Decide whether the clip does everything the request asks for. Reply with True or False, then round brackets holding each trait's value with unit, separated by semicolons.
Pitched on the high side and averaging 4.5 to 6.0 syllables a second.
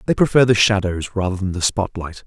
False (100 Hz; 5.7 syllables/s)